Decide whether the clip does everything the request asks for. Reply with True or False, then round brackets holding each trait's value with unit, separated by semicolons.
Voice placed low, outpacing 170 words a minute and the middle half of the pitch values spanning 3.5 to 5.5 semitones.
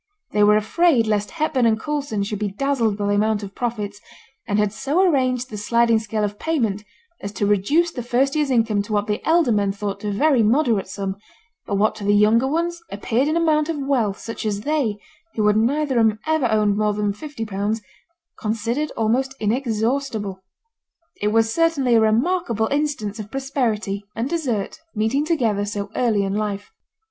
False (225 Hz; 190 wpm; 4.7 semitones)